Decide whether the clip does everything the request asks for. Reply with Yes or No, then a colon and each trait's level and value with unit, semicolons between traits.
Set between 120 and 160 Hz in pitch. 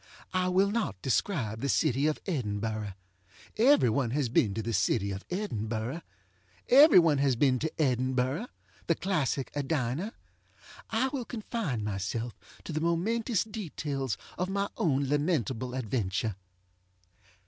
Yes: medium, 140 Hz